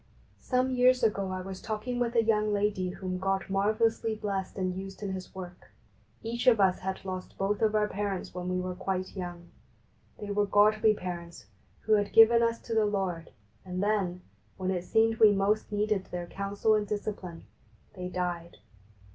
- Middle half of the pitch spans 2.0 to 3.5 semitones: Yes, average, 2.7 semitones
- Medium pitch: No, high, 200 Hz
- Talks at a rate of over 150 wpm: Yes, average, 180 wpm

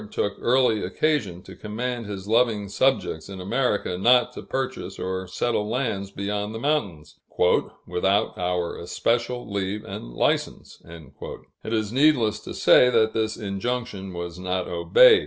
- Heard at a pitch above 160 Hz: No, low, 105 Hz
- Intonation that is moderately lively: Yes, average, 4.6 semitones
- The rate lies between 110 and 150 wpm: Yes, average, 140 wpm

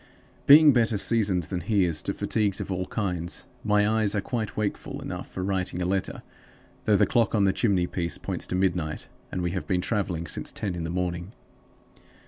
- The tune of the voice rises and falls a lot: No, average, 3.0 semitones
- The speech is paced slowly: No, average, 200 wpm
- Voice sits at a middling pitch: No, very low, 95 Hz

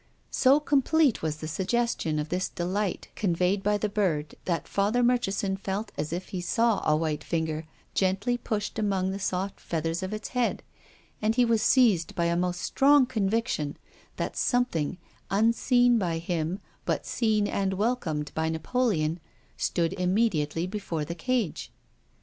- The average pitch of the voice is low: No, high, 195 Hz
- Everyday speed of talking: Yes, average, 160 wpm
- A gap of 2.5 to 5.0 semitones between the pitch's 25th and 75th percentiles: No, wide, 5.4 semitones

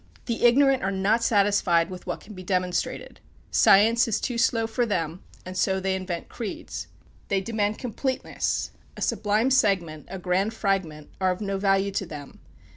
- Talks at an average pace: Yes, average, 170 wpm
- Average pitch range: Yes, average, 3.4 semitones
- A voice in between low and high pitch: No, high, 195 Hz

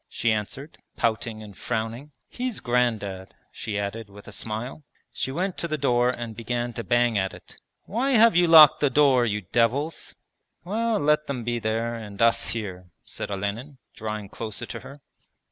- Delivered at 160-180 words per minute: Yes, average, 175 wpm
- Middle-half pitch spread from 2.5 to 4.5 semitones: No, average, 5.1 semitones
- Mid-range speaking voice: No, low, 120 Hz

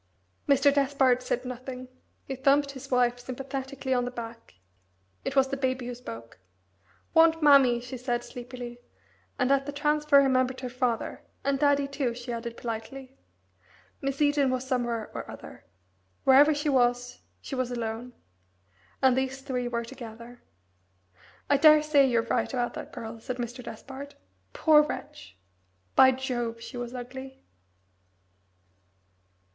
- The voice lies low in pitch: No, very high, 255 Hz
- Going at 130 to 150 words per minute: Yes, average, 140 wpm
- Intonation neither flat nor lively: No, narrow, 2.1 semitones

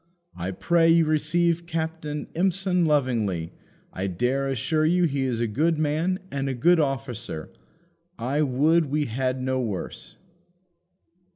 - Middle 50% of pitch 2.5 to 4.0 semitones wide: No, average, 4.6 semitones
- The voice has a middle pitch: Yes, medium, 145 Hz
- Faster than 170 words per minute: No, slow, 135 wpm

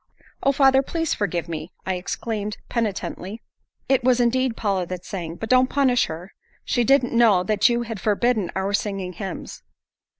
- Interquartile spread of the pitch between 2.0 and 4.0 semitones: No, average, 4.7 semitones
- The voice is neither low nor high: No, high, 215 Hz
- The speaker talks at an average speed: Yes, average, 165 wpm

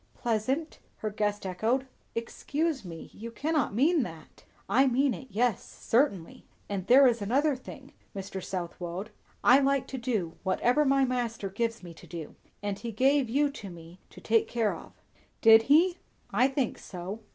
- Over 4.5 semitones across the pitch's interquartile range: Yes, wide, 5.5 semitones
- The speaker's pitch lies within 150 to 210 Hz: No, high, 230 Hz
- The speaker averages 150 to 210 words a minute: Yes, average, 165 wpm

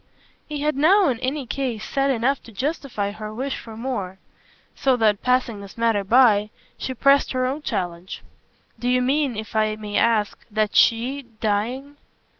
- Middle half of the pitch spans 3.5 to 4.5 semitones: Yes, average, 4.1 semitones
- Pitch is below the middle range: No, high, 240 Hz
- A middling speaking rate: Yes, average, 170 wpm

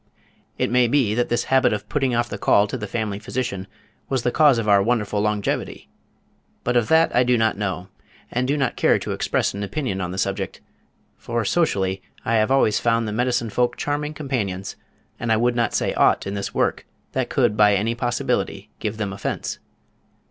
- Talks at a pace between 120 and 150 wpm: No, average, 200 wpm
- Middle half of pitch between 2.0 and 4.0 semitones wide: Yes, average, 3.4 semitones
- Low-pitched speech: Yes, low, 115 Hz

